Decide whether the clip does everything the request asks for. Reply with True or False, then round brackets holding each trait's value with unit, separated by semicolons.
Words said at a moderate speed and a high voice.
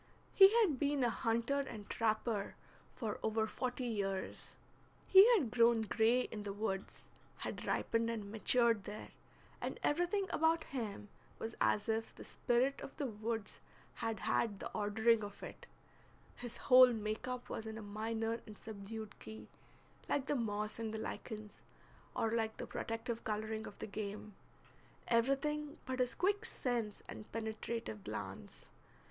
True (155 wpm; 225 Hz)